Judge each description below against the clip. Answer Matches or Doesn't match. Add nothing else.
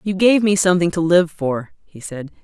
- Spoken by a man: Doesn't match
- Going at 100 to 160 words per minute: Doesn't match